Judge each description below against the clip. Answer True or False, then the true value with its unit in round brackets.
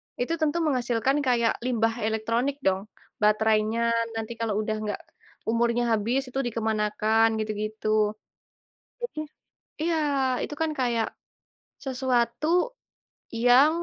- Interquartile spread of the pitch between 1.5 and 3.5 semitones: True (2.8 semitones)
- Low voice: False (230 Hz)